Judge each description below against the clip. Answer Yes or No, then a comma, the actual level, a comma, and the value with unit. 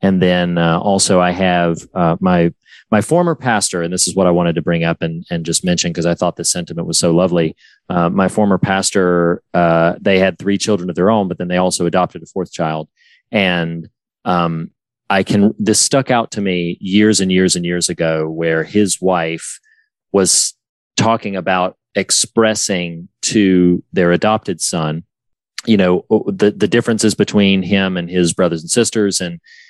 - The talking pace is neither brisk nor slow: Yes, average, 185 wpm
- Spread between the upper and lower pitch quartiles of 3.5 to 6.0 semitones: No, average, 3.0 semitones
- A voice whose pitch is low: Yes, very low, 90 Hz